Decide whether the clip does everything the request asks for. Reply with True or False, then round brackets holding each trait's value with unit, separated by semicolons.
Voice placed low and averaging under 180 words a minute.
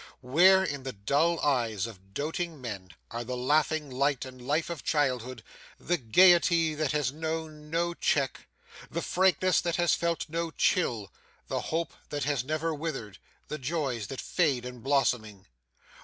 False (145 Hz; 155 wpm)